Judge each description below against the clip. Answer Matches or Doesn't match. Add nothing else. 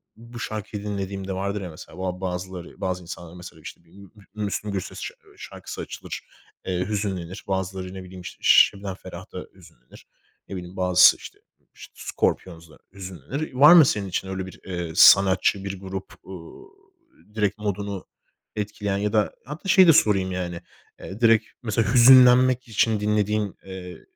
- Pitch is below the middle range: Matches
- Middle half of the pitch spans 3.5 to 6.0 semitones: Doesn't match